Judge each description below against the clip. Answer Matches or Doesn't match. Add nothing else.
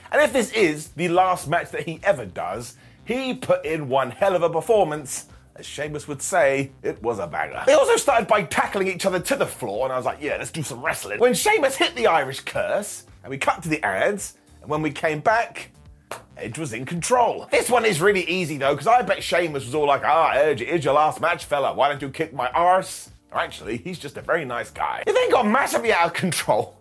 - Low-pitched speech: Doesn't match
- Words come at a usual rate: Doesn't match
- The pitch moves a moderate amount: Doesn't match